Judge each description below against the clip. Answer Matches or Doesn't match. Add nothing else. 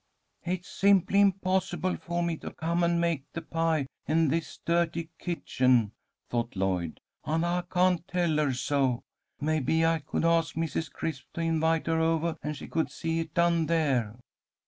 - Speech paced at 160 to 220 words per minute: Matches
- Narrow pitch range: Matches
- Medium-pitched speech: Matches